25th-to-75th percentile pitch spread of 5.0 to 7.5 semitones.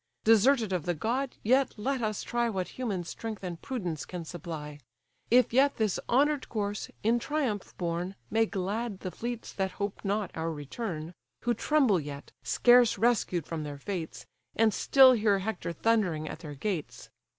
Yes: wide, 5.4 semitones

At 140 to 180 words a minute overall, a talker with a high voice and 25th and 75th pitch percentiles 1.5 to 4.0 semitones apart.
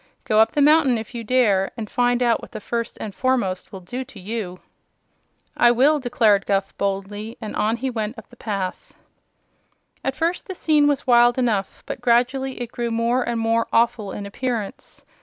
No: average, 190 wpm; high, 235 Hz; average, 3.2 semitones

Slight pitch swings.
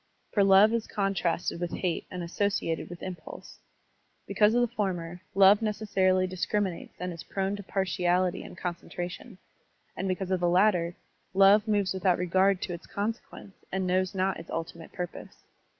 Yes: narrow, 2.2 semitones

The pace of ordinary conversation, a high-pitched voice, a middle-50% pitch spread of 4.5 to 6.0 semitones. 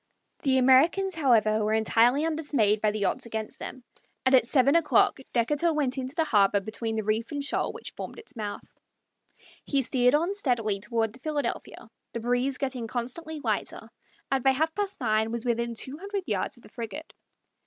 Yes: average, 185 wpm; very high, 255 Hz; average, 4.9 semitones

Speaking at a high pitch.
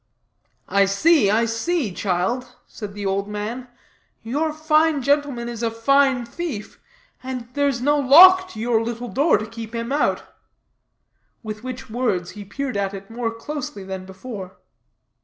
Yes: high, 235 Hz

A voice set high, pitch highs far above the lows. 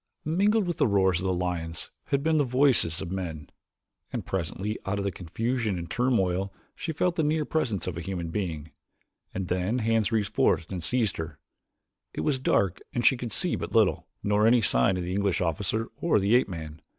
No: low, 100 Hz; wide, 5.8 semitones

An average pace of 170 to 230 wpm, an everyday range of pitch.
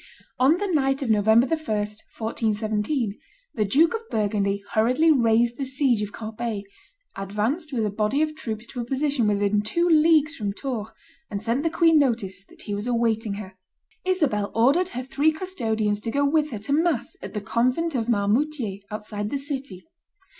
No: average, 175 wpm; wide, 5.7 semitones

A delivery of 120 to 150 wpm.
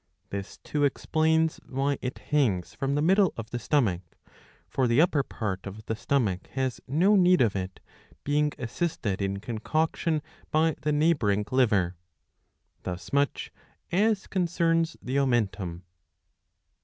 Yes: slow, 135 wpm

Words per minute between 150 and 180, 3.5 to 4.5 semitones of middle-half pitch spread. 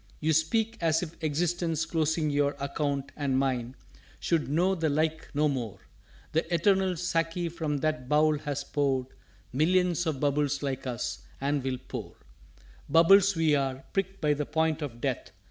No: average, 160 wpm; average, 3.0 semitones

